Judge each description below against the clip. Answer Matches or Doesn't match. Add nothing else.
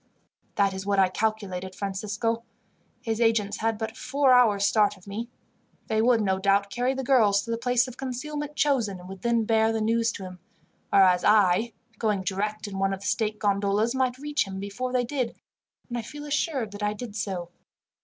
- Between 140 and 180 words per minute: Doesn't match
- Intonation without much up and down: Doesn't match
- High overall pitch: Matches